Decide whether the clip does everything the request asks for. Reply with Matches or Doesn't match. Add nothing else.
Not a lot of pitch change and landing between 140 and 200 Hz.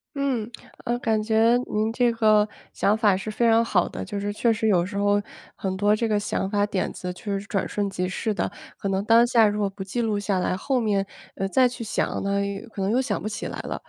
Doesn't match